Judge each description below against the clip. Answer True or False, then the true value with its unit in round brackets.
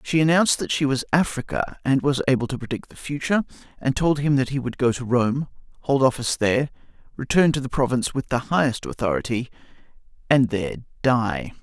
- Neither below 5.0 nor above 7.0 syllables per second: True (6.0 syllables/s)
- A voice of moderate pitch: False (130 Hz)